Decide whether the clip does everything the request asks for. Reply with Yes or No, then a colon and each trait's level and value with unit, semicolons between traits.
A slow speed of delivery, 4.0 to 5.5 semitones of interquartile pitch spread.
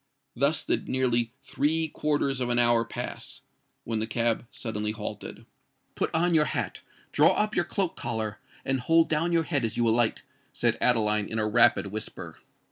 No: average, 165 wpm; average, 5.2 semitones